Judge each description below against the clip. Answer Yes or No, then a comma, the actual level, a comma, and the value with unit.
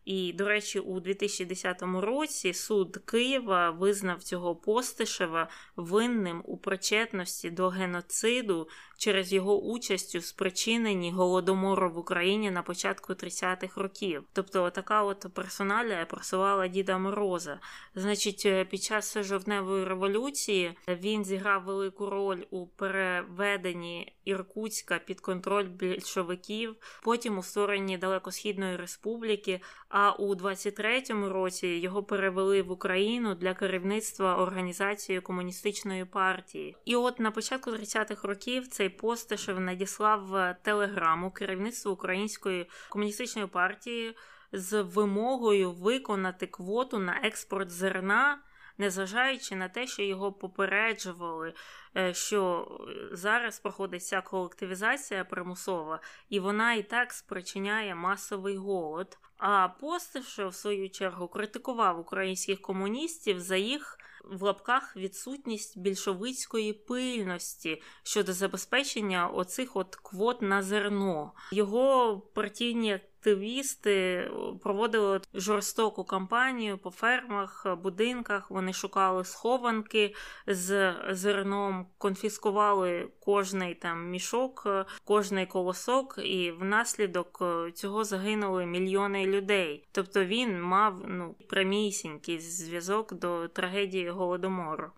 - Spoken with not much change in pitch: Yes, narrow, 2.3 semitones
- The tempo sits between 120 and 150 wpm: No, slow, 105 wpm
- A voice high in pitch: Yes, high, 195 Hz